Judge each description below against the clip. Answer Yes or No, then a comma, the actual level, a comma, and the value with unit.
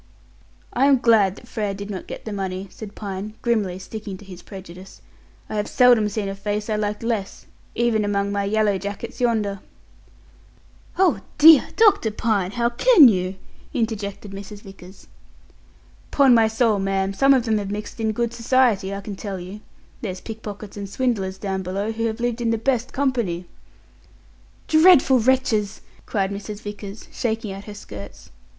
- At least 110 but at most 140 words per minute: No, average, 170 wpm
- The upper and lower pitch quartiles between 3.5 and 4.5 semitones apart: No, average, 3.0 semitones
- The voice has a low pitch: No, high, 210 Hz